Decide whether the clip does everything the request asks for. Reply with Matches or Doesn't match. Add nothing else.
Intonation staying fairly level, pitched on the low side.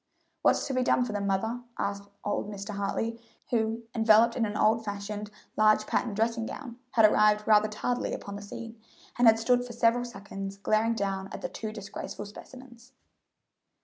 Doesn't match